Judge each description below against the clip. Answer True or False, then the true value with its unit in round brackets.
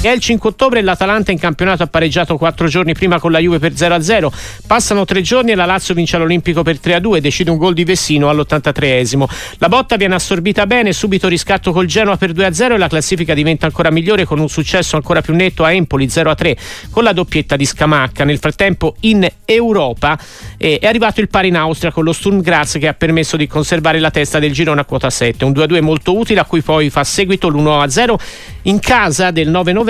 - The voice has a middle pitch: True (170 Hz)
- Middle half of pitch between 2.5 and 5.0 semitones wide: True (3.8 semitones)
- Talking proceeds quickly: True (215 wpm)